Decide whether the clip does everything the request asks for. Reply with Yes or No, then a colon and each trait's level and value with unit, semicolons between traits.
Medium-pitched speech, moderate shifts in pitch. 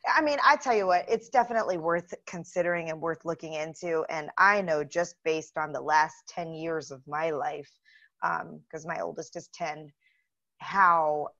No: medium, 165 Hz; narrow, 2.2 semitones